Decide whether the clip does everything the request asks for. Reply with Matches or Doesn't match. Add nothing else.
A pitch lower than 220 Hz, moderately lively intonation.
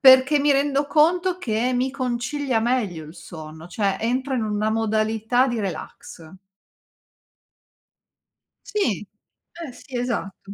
Doesn't match